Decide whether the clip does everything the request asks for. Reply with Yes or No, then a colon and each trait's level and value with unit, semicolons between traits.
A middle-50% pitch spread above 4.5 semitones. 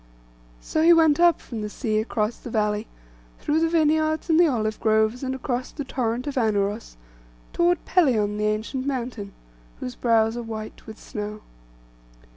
Yes: wide, 5.5 semitones